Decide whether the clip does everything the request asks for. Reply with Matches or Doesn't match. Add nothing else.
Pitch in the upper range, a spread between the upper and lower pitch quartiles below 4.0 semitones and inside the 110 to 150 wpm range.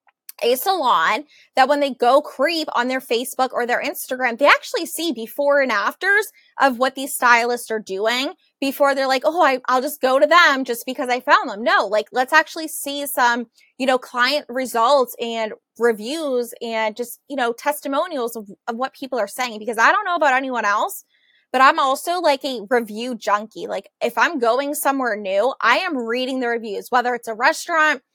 Doesn't match